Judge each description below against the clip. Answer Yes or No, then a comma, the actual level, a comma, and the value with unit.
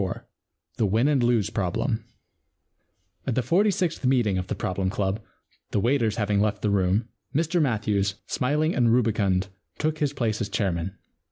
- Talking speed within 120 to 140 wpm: No, average, 165 wpm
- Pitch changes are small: No, average, 4.9 semitones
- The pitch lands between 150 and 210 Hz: No, low, 110 Hz